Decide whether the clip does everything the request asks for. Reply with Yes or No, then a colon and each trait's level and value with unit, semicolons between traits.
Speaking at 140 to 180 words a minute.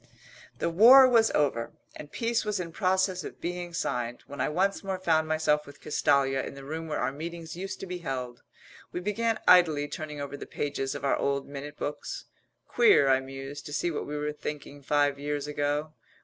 No: average, 200 wpm